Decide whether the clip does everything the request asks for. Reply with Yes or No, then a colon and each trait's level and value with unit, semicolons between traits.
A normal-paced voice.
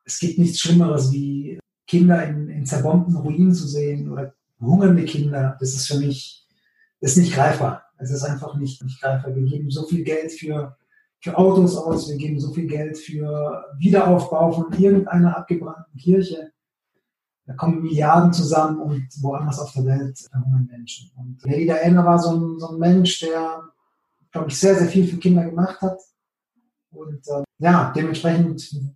Yes: average, 175 wpm